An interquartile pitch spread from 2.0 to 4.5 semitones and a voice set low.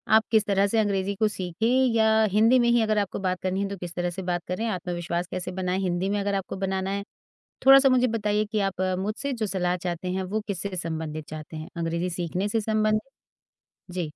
No: average, 3.2 semitones; high, 195 Hz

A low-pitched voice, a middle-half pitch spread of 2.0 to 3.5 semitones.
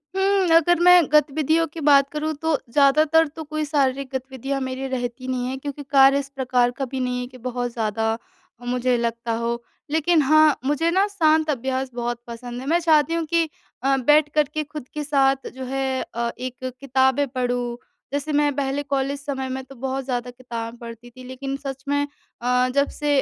No: very high, 270 Hz; average, 3.1 semitones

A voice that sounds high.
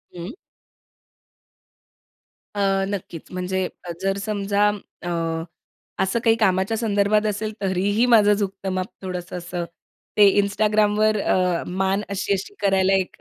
Yes: high, 200 Hz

